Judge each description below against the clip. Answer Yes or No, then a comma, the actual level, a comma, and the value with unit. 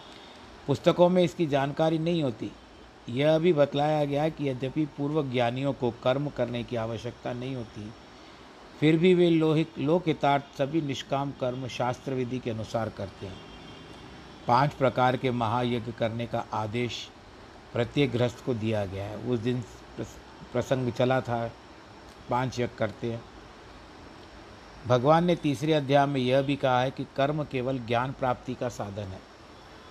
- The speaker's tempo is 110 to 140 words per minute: No, average, 150 wpm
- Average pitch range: Yes, average, 3.2 semitones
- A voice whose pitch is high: No, low, 125 Hz